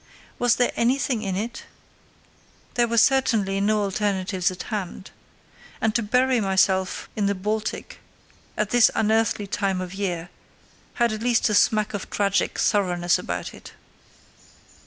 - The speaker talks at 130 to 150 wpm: Yes, average, 140 wpm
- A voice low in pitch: No, high, 210 Hz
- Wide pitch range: No, average, 3.0 semitones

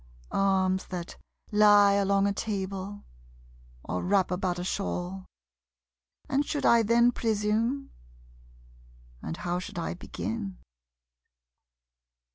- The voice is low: No, high, 200 Hz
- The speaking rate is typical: No, slow, 100 wpm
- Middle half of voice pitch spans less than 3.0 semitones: Yes, narrow, 2.5 semitones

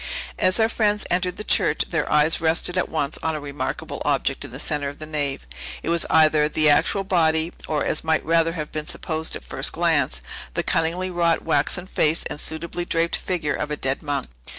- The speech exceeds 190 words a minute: Yes, fast, 205 wpm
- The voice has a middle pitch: Yes, medium, 160 Hz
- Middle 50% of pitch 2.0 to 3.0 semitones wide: Yes, narrow, 2.4 semitones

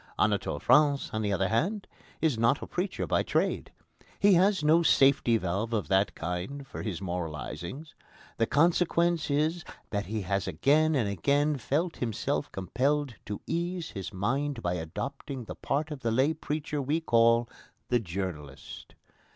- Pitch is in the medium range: No, low, 130 Hz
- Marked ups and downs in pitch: Yes, wide, 7.3 semitones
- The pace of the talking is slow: No, average, 160 wpm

